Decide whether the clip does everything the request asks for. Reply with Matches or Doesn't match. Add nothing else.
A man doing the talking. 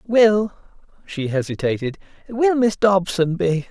Matches